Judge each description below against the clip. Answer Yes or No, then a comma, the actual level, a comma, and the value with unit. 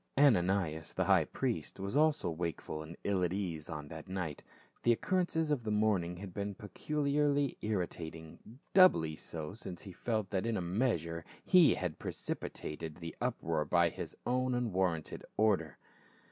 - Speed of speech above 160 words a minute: No, average, 155 wpm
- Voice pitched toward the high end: No, very low, 95 Hz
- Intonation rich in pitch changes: Yes, wide, 6.3 semitones